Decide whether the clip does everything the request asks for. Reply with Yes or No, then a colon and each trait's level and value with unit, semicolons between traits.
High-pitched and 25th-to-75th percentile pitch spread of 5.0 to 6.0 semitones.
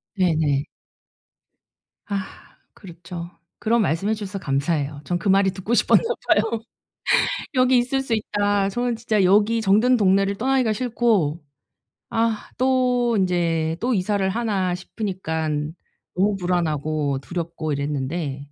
Yes: high, 195 Hz; average, 5.3 semitones